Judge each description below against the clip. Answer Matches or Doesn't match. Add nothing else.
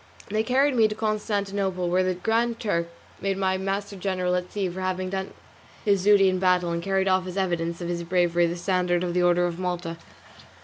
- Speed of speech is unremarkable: Doesn't match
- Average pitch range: Doesn't match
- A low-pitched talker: Doesn't match